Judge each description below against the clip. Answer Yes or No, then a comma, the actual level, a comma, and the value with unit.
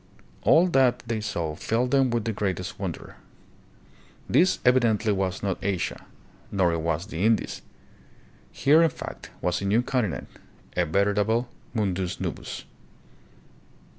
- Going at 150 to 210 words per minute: No, slow, 135 wpm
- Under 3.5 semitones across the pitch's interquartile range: No, average, 4.6 semitones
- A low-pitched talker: Yes, low, 105 Hz